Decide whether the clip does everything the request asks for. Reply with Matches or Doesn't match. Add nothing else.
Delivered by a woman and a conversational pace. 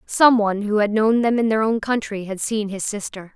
Doesn't match